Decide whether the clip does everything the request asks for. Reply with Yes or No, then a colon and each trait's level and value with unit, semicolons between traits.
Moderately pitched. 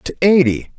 Yes: medium, 160 Hz